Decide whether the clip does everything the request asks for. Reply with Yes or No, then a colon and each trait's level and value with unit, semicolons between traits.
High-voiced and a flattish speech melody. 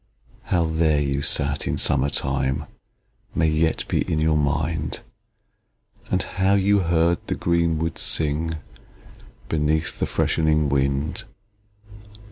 No: very low, 80 Hz; narrow, 2.3 semitones